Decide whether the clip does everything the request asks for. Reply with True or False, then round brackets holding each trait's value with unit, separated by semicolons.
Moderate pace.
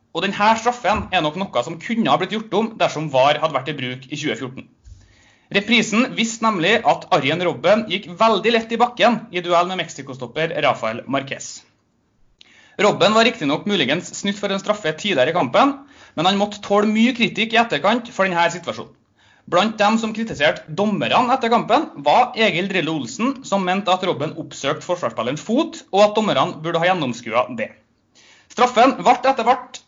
True (175 wpm)